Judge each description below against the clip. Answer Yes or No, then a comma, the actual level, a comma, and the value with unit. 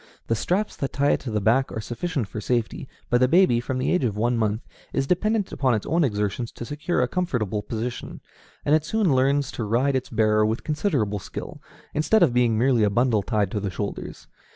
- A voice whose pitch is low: Yes, low, 125 Hz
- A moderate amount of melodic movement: Yes, average, 5.0 semitones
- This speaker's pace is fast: Yes, fast, 220 wpm